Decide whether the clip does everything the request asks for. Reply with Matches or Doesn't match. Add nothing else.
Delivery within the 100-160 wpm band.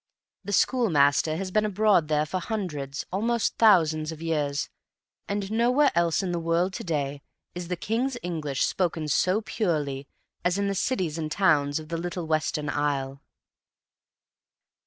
Matches